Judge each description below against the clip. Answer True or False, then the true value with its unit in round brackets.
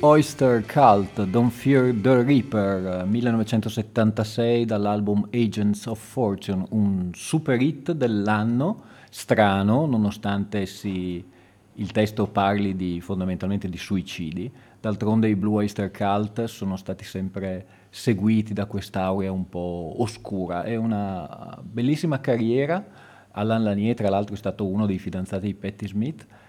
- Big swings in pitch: False (3.0 semitones)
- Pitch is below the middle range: True (105 Hz)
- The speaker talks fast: False (125 wpm)